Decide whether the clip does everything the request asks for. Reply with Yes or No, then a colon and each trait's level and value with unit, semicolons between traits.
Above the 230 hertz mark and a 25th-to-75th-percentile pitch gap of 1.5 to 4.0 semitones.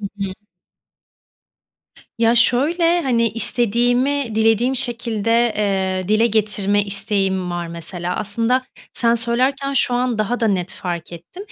No: high, 225 Hz; average, 3.7 semitones